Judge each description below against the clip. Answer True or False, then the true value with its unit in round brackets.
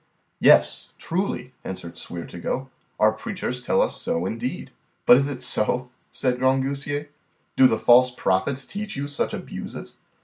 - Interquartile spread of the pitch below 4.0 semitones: True (2.7 semitones)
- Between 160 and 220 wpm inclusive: False (150 wpm)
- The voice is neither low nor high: False (130 Hz)